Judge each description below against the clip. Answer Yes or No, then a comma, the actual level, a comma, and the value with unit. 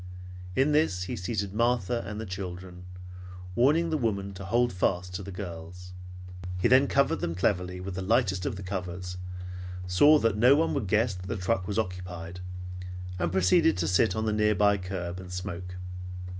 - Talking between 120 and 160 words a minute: No, average, 180 wpm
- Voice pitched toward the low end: Yes, very low, 95 Hz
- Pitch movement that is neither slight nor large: Yes, average, 3.7 semitones